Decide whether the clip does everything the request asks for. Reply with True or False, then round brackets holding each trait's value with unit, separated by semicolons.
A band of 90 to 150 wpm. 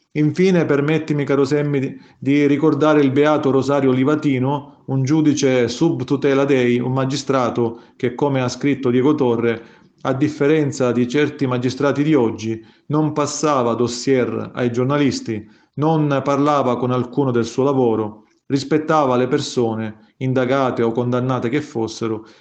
True (130 wpm)